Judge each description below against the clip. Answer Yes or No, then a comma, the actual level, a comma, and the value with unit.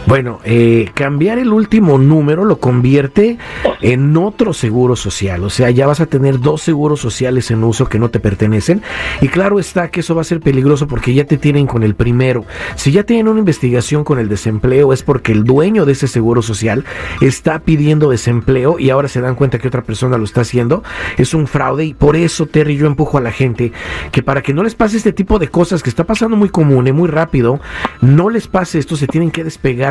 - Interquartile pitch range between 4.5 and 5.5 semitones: Yes, average, 4.9 semitones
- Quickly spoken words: Yes, fast, 225 wpm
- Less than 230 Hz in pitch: Yes, medium, 140 Hz